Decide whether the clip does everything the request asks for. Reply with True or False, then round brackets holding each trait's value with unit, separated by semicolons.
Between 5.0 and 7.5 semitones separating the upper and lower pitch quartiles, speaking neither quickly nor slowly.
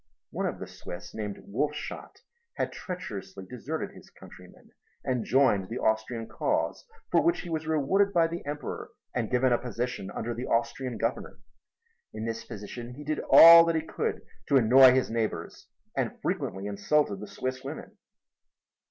True (5.3 semitones; 160 wpm)